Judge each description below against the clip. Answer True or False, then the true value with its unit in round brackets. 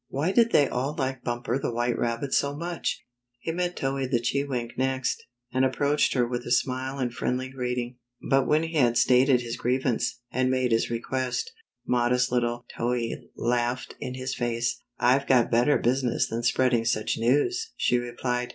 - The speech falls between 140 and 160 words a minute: False (180 wpm)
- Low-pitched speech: True (125 Hz)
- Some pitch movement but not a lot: False (1.9 semitones)